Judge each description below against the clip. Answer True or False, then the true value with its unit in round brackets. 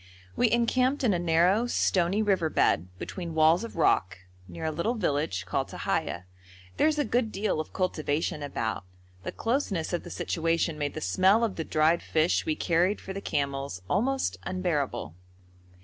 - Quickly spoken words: False (170 wpm)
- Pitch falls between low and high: True (170 Hz)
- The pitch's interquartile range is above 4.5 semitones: True (5.4 semitones)